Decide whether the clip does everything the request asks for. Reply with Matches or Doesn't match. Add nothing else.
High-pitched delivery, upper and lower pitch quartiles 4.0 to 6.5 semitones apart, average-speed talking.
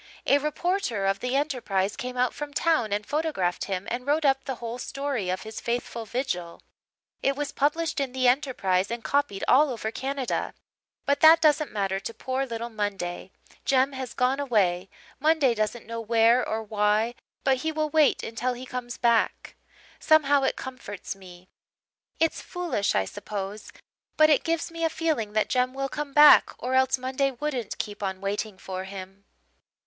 Matches